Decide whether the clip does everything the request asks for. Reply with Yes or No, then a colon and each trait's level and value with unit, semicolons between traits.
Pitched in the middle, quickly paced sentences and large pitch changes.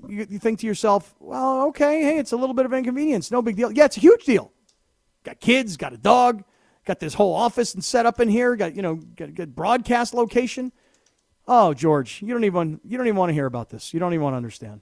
No: high, 225 Hz; fast, 255 wpm; wide, 5.7 semitones